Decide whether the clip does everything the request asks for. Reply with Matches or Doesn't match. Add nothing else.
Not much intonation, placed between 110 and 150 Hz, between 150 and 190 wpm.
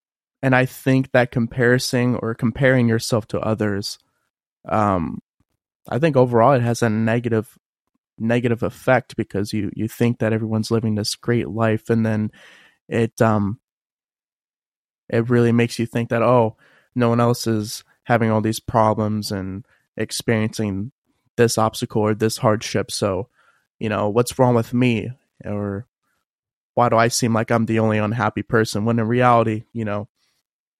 Matches